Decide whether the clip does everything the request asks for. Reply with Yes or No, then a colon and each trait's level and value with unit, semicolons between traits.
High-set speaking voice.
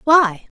Yes: very high, 260 Hz